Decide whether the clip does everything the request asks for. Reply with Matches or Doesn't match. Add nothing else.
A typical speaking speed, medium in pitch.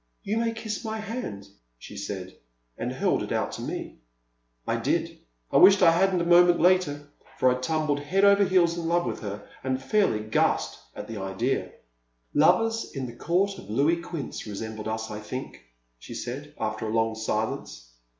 Matches